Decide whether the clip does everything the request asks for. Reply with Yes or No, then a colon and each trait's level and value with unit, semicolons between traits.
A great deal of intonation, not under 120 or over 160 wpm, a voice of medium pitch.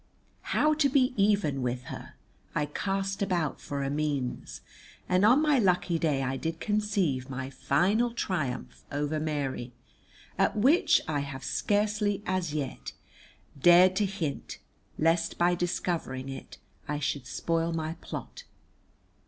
Yes: wide, 6.1 semitones; slow, 135 wpm; medium, 165 Hz